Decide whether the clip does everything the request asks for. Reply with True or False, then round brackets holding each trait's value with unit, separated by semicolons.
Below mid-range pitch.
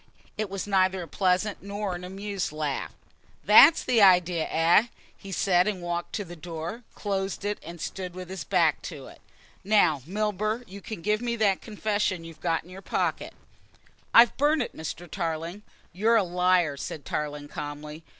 False (185 Hz)